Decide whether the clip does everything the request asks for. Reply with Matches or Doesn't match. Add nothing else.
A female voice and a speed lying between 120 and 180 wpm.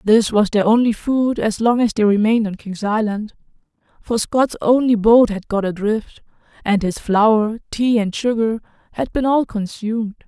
Matches